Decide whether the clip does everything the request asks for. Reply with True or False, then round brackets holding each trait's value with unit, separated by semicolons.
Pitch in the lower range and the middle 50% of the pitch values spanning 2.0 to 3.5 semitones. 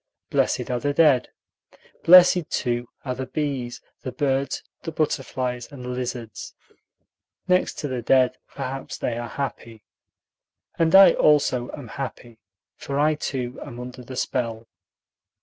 True (130 Hz; 2.9 semitones)